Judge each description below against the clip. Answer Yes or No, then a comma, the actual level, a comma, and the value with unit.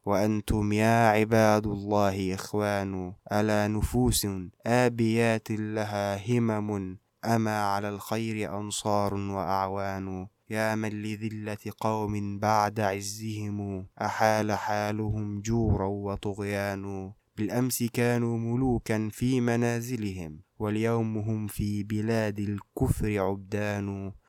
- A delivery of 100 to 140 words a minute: No, average, 90 wpm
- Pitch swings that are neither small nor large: No, narrow, 1.6 semitones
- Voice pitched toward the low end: Yes, low, 105 Hz